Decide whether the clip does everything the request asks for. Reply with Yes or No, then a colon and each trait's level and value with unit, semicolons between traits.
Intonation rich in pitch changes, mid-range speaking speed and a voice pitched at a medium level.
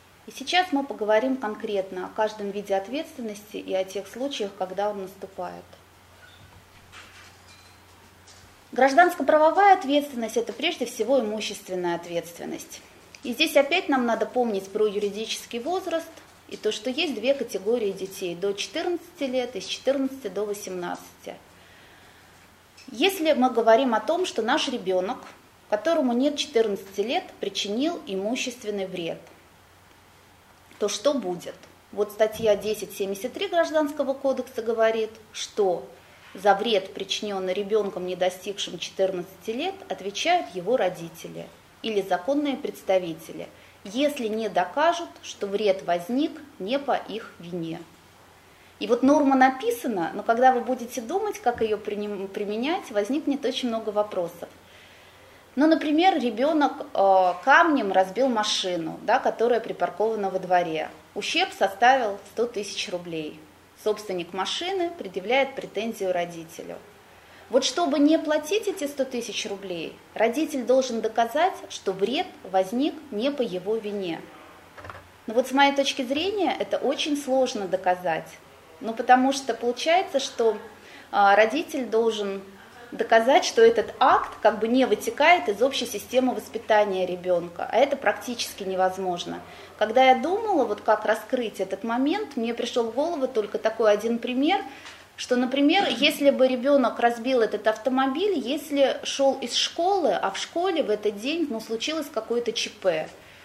No: wide, 6.2 semitones; average, 130 wpm; high, 220 Hz